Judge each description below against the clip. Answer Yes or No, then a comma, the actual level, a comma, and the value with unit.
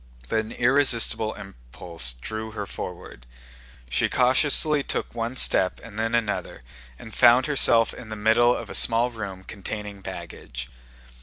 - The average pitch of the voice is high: No, low, 110 Hz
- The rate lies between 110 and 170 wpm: Yes, average, 145 wpm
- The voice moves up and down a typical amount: Yes, average, 3.6 semitones